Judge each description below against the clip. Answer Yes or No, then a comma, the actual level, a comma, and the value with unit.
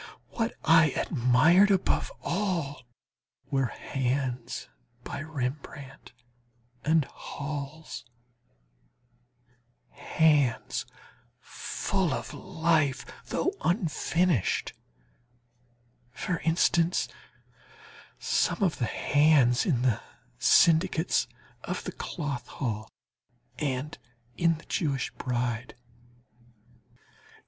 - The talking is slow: Yes, slow, 75 wpm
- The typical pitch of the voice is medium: Yes, medium, 150 Hz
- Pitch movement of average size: Yes, average, 4.4 semitones